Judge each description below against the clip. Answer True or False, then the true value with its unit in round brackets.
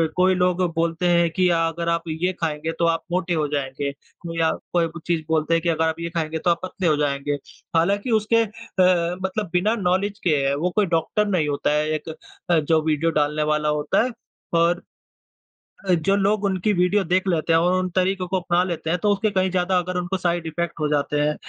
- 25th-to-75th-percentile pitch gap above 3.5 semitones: False (2.6 semitones)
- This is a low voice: False (170 Hz)